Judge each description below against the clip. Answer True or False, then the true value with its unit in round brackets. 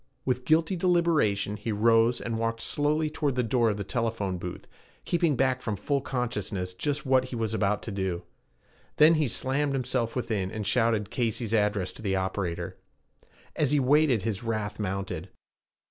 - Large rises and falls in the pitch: False (4.6 semitones)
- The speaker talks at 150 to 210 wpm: True (170 wpm)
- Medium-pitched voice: False (115 Hz)